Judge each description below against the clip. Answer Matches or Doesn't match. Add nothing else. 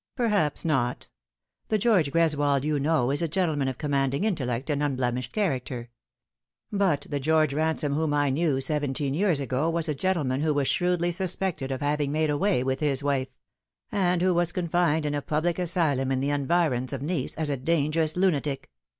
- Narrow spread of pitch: Doesn't match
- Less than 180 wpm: Doesn't match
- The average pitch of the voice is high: Doesn't match